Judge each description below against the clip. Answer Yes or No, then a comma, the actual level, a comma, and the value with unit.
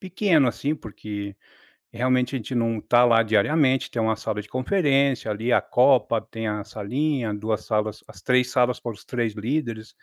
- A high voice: No, low, 120 Hz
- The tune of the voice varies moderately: Yes, average, 3.1 semitones